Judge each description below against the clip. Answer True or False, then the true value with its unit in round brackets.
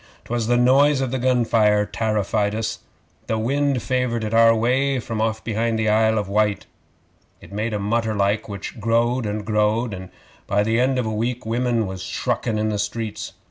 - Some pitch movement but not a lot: False (2.2 semitones)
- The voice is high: False (110 Hz)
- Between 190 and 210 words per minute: True (195 wpm)